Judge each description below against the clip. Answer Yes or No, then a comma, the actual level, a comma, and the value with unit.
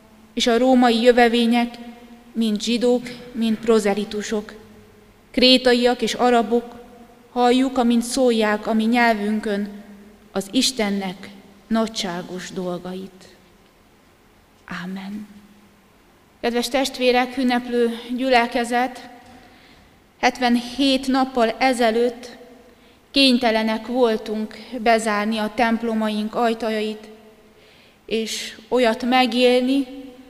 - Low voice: No, high, 235 Hz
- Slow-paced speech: Yes, slow, 75 wpm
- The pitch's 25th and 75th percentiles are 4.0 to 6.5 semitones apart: No, narrow, 2.4 semitones